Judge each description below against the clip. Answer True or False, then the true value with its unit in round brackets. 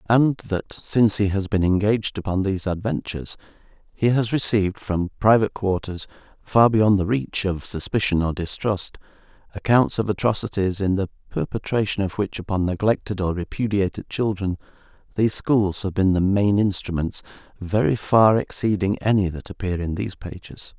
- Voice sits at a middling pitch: False (100 Hz)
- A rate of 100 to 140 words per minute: False (155 wpm)